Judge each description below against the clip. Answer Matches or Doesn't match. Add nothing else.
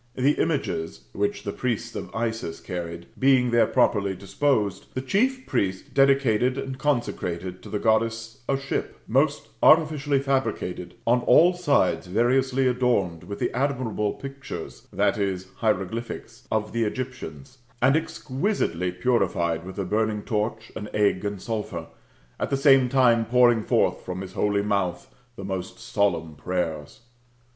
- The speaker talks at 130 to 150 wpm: Matches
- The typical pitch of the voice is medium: Doesn't match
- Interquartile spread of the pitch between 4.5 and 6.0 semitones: Matches